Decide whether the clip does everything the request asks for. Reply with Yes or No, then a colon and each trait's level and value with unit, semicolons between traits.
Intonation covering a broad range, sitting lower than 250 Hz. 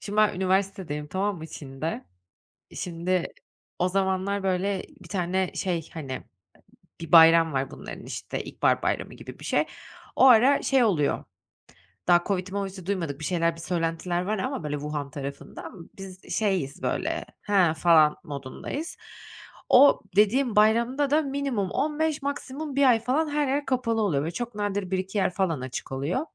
Yes: wide, 5.7 semitones; high, 190 Hz